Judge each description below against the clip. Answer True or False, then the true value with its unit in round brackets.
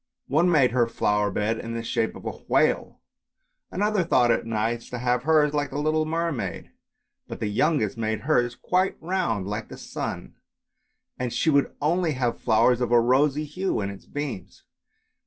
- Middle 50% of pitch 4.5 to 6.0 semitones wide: True (5.3 semitones)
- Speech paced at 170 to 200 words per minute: True (175 wpm)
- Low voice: True (125 Hz)